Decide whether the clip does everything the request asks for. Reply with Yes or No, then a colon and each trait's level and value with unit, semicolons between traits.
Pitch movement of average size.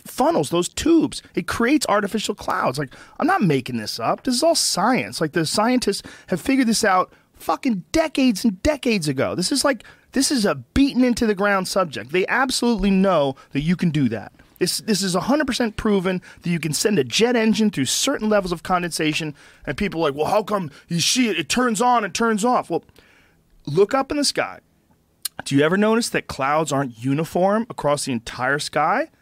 No: wide, 6.9 semitones